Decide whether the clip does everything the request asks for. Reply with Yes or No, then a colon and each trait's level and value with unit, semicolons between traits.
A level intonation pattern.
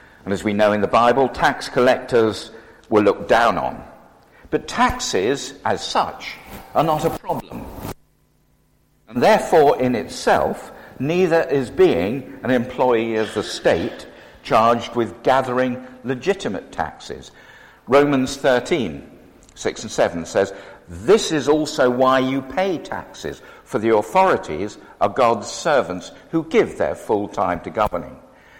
No: average, 4.6 semitones